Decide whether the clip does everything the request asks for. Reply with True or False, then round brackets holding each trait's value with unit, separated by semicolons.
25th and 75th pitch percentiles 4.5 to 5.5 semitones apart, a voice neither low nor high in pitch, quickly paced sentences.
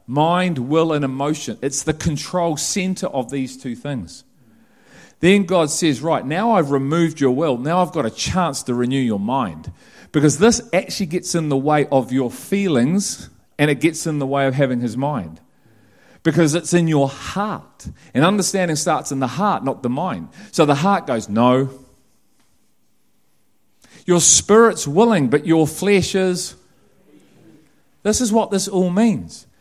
False (5.2 semitones; 160 Hz; 165 wpm)